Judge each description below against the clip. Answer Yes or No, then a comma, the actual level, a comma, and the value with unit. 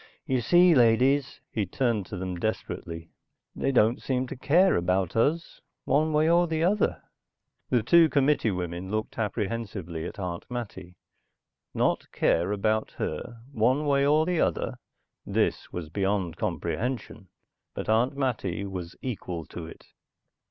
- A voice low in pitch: Yes, low, 115 Hz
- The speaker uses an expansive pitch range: Yes, wide, 6.8 semitones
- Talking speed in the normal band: Yes, average, 145 wpm